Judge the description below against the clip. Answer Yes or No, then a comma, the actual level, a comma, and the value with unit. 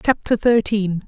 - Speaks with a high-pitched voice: Yes, high, 210 Hz